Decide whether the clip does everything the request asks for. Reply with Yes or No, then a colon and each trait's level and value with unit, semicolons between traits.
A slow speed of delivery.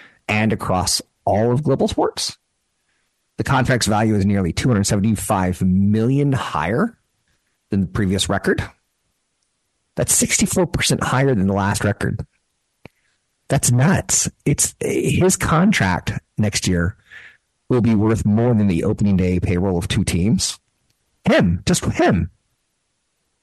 Yes: slow, 120 wpm